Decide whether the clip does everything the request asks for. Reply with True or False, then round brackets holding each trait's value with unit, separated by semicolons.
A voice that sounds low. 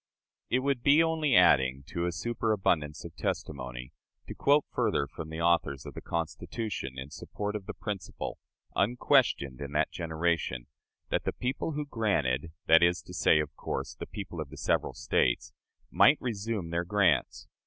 True (85 Hz)